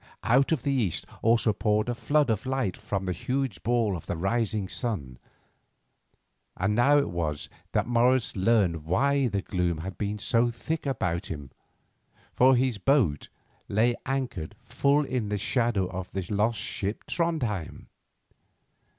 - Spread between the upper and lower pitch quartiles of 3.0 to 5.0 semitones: No, wide, 5.4 semitones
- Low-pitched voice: Yes, low, 110 Hz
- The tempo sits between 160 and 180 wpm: No, average, 150 wpm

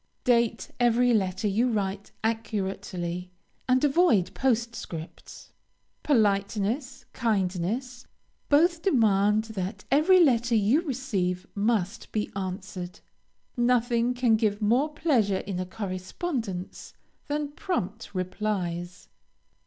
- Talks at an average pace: No, slow, 100 wpm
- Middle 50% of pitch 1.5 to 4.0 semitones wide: No, average, 4.5 semitones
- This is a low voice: No, high, 220 Hz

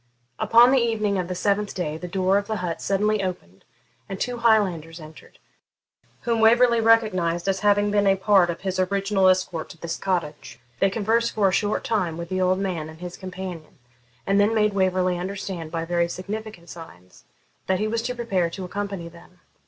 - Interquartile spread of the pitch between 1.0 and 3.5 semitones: Yes, average, 3.2 semitones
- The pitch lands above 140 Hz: Yes, high, 190 Hz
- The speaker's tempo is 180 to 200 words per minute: Yes, average, 190 wpm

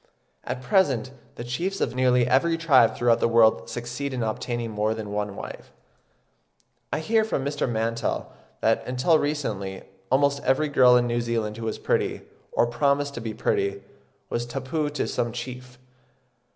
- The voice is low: Yes, low, 125 Hz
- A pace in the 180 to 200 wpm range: No, average, 165 wpm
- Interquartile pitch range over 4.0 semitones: No, average, 3.6 semitones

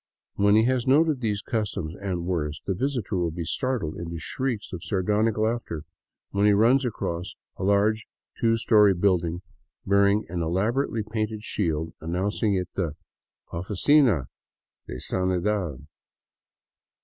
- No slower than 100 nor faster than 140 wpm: Yes, slow, 135 wpm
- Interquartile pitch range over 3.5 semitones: Yes, average, 4.1 semitones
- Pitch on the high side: No, low, 100 Hz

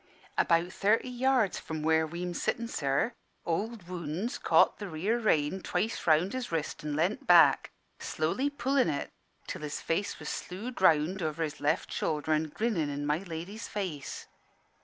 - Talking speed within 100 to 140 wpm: No, average, 160 wpm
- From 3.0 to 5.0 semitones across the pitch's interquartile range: No, wide, 5.6 semitones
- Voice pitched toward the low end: No, medium, 175 Hz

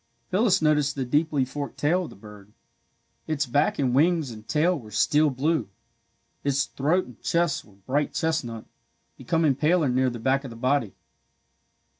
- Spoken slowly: No, average, 165 wpm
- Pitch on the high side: No, medium, 140 Hz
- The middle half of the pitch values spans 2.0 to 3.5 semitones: No, average, 4.1 semitones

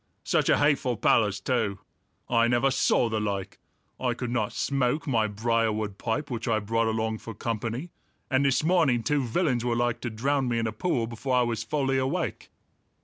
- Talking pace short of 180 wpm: No, average, 190 wpm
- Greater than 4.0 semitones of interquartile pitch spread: No, average, 3.1 semitones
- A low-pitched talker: Yes, low, 120 Hz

